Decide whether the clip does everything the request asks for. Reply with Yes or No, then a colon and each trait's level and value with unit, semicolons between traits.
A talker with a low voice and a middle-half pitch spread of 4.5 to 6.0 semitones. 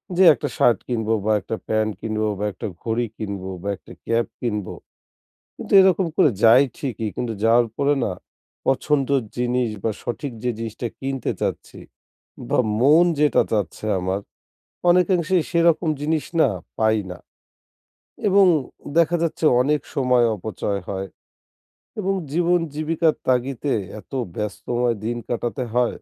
Yes: low, 125 Hz; wide, 5.5 semitones